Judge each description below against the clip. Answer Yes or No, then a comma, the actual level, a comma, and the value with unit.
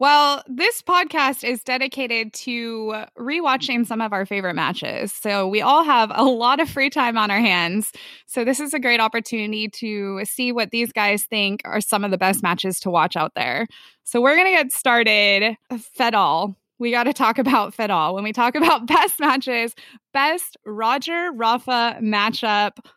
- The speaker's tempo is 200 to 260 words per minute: No, average, 185 wpm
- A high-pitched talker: Yes, high, 235 Hz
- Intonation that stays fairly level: No, average, 4.1 semitones